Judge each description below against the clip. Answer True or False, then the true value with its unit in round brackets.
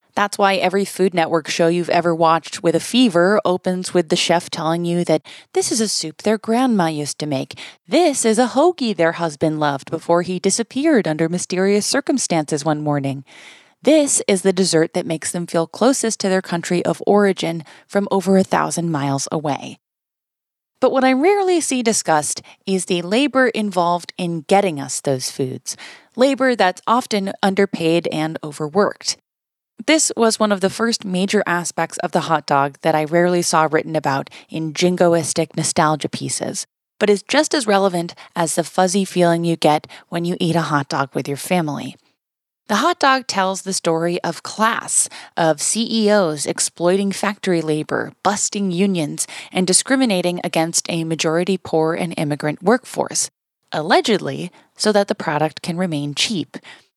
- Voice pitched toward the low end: False (180 Hz)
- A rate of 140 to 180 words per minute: True (165 wpm)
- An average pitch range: True (4.2 semitones)